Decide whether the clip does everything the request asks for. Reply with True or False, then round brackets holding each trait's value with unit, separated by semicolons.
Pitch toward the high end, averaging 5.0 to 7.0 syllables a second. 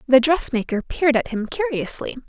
True (270 Hz; 5.7 syllables/s)